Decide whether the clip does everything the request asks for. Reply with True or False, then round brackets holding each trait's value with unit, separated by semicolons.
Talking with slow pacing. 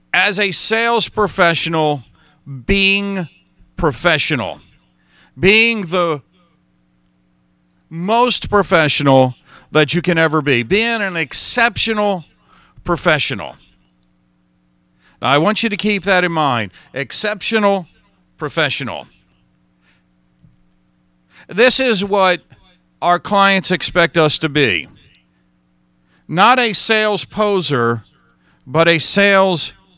True (90 wpm)